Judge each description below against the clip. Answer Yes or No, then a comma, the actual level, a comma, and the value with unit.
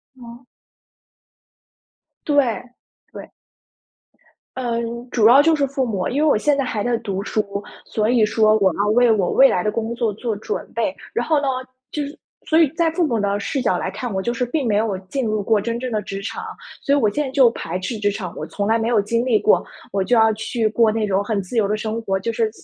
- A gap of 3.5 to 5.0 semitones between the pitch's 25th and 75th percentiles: No, average, 3.1 semitones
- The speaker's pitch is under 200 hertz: No, high, 225 Hz